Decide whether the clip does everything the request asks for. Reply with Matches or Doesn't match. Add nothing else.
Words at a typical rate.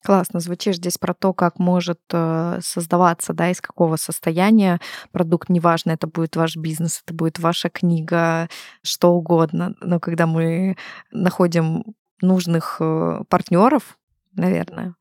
Matches